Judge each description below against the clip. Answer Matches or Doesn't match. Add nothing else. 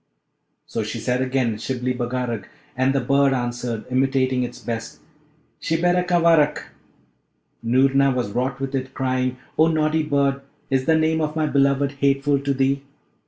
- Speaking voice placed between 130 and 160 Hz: Matches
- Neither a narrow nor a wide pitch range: Doesn't match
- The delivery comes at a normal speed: Matches